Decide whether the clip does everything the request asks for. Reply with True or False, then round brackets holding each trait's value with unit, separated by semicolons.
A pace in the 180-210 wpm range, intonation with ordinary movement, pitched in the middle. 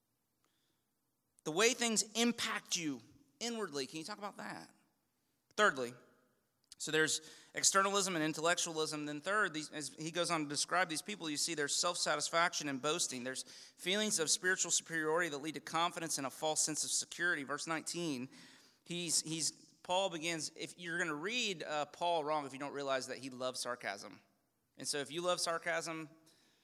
False (170 wpm; 3.4 semitones; 160 Hz)